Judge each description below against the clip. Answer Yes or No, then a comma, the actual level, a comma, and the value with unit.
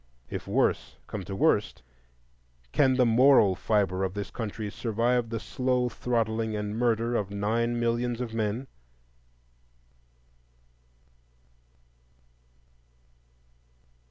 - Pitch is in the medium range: No, low, 115 Hz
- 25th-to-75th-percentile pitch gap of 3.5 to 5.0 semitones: No, average, 2.7 semitones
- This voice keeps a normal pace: No, slow, 100 wpm